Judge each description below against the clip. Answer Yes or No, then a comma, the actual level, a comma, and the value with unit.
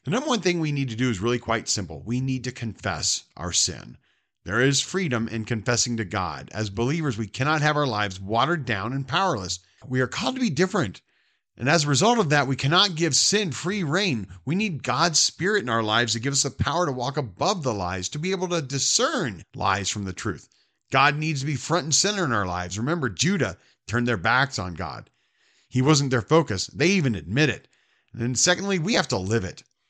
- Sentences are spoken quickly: Yes, fast, 225 wpm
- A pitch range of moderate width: No, wide, 6.4 semitones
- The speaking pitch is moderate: No, low, 130 Hz